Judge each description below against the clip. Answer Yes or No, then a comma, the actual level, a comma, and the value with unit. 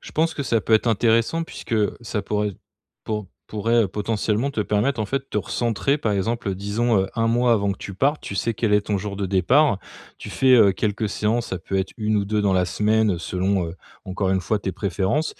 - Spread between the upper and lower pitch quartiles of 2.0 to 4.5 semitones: Yes, average, 2.8 semitones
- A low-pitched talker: Yes, low, 105 Hz